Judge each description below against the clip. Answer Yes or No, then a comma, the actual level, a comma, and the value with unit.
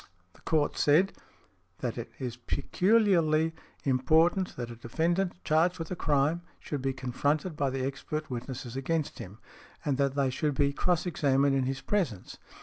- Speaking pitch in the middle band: Yes, medium, 145 Hz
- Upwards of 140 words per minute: Yes, average, 160 wpm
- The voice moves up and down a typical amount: Yes, average, 3.8 semitones